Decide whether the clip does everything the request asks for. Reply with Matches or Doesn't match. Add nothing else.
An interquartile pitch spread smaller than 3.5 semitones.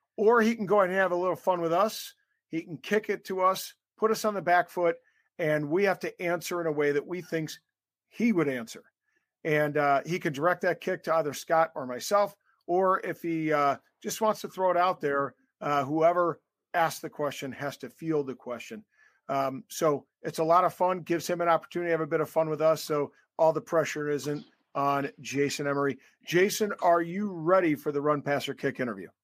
Doesn't match